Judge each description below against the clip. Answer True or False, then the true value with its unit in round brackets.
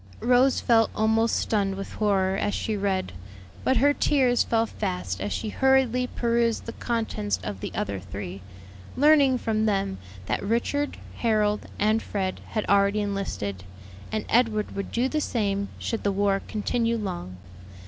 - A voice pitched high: True (215 Hz)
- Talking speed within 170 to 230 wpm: False (155 wpm)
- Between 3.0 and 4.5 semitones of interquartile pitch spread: True (3.3 semitones)